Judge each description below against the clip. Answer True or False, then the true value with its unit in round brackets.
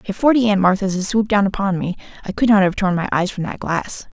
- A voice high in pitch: True (195 Hz)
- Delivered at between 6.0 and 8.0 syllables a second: True (6.2 syllables/s)